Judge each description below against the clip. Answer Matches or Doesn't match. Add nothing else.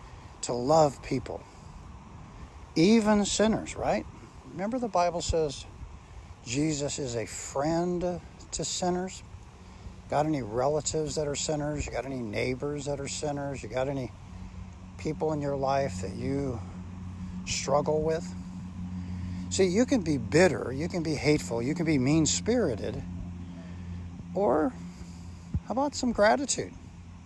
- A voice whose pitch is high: Doesn't match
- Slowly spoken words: Matches